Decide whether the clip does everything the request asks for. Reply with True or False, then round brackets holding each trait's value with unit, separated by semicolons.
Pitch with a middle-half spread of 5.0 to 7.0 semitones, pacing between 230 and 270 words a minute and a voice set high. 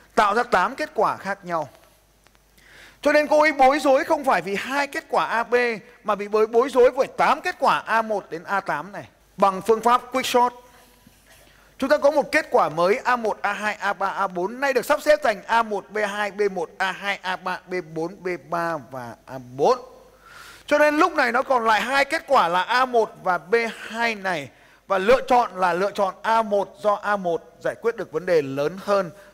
False (5.5 semitones; 190 wpm; 220 Hz)